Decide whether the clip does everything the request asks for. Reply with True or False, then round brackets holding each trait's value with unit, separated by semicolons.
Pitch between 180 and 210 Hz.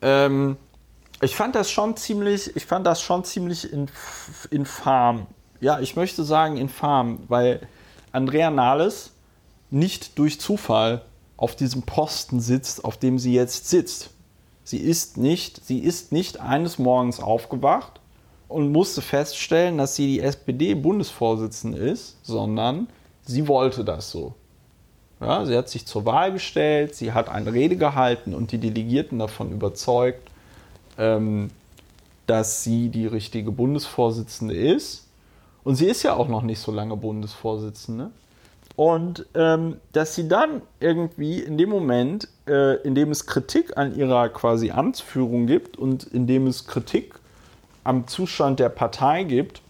False (130 Hz)